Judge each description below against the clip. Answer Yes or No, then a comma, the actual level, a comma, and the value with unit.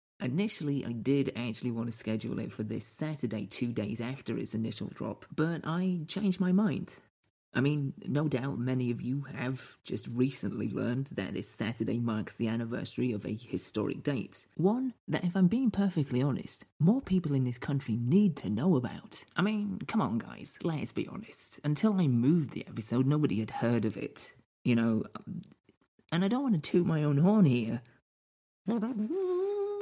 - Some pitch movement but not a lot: No, wide, 7.6 semitones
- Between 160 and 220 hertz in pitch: No, low, 135 Hz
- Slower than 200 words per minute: Yes, average, 180 wpm